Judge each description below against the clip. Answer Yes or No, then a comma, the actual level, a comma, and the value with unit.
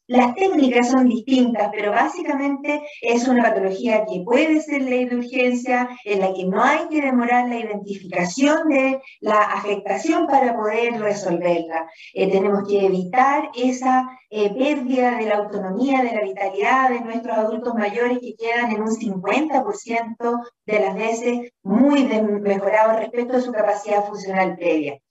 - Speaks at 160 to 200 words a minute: No, average, 150 wpm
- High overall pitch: Yes, high, 235 Hz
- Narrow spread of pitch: No, average, 3.8 semitones